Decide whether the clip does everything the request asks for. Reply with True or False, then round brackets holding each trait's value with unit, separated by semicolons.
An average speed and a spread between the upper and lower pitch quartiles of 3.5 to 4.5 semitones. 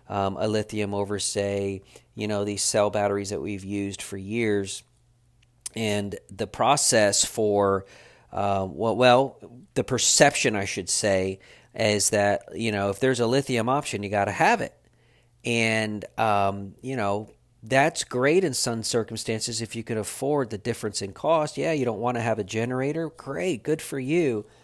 False (170 wpm; 3.0 semitones)